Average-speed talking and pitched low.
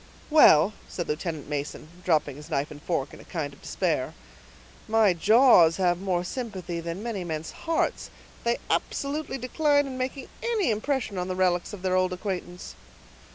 No: average, 160 wpm; medium, 185 Hz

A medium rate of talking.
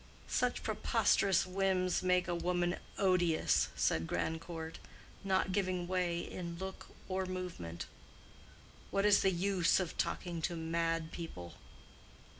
No: slow, 120 wpm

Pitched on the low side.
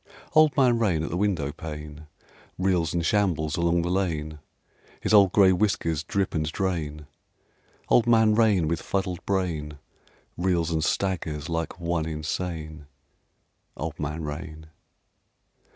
Yes: very low, 85 Hz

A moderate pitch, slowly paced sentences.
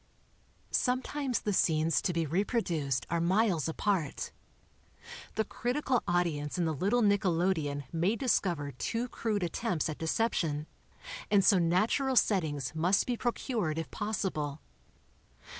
Yes: medium, 180 Hz; slow, 125 wpm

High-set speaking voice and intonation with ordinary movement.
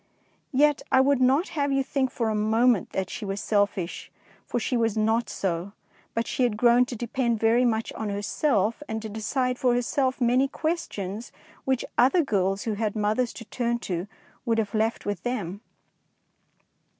Yes: high, 230 Hz; average, 3.4 semitones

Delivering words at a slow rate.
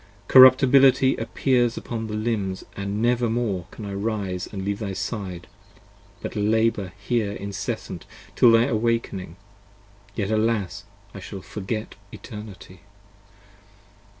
Yes: slow, 125 wpm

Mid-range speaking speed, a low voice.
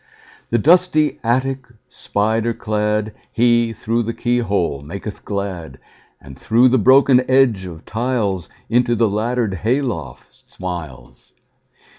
No: slow, 105 wpm; low, 115 Hz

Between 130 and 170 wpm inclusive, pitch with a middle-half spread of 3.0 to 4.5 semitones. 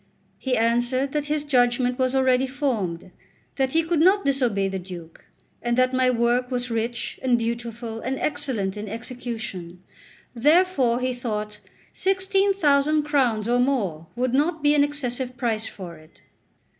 Yes: average, 155 wpm; average, 3.7 semitones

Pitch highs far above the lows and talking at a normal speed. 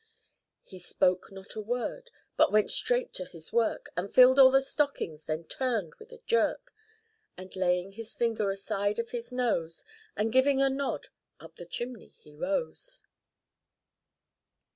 Yes: wide, 6.2 semitones; average, 155 wpm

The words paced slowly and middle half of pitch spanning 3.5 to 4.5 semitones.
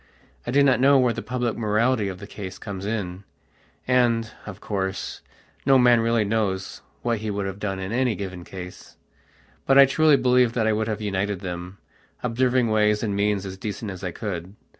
No: average, 195 wpm; average, 3.8 semitones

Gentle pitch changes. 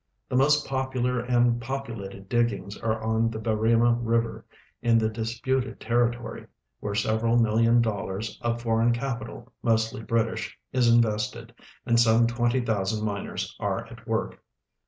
Yes: narrow, 1.4 semitones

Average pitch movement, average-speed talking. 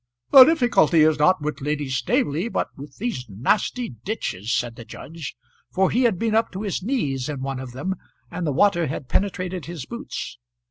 No: wide, 7.6 semitones; average, 190 wpm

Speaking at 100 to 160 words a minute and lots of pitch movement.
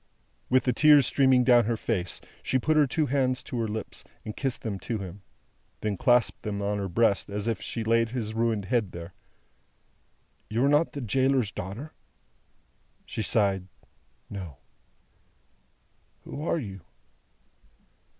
No: average, 150 wpm; average, 4.2 semitones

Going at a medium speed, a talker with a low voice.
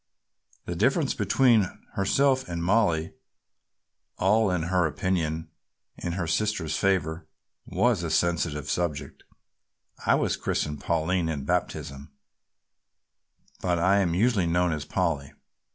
No: slow, 120 wpm; very low, 85 Hz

